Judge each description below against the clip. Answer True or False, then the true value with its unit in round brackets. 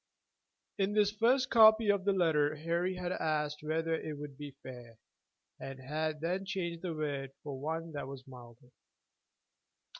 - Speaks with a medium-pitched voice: True (155 Hz)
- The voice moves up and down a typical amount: True (4.6 semitones)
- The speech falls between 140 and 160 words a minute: True (155 wpm)